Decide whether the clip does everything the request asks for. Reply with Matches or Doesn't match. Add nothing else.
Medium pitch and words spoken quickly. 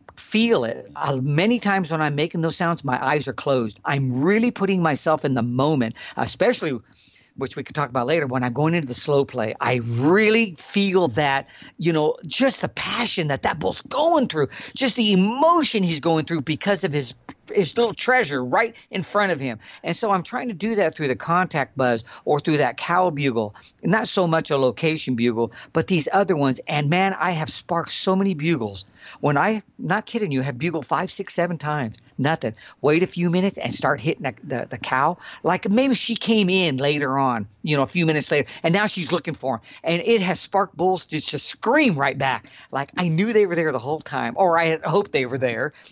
Matches